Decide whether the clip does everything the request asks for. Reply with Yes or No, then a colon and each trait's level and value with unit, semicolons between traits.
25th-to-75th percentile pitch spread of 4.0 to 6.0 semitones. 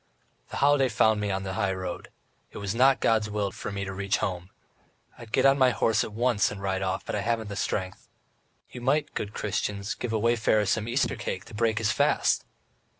No: average, 3.0 semitones